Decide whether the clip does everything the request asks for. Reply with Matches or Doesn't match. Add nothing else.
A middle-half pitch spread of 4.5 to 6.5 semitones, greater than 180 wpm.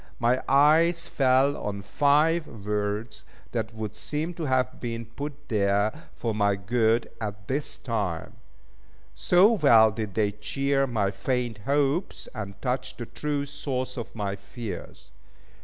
Doesn't match